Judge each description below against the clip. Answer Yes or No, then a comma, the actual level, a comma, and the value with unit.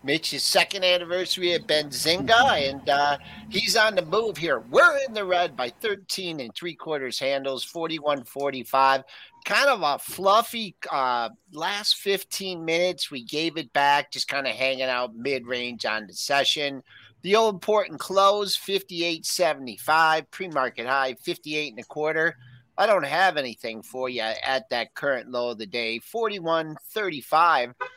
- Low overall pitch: No, medium, 155 Hz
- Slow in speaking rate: No, average, 155 wpm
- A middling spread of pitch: No, wide, 5.8 semitones